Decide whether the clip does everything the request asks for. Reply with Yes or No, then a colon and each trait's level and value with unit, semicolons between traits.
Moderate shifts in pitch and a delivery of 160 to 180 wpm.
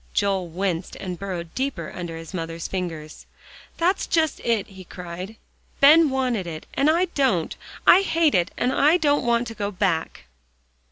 No: wide, 8.2 semitones; average, 165 wpm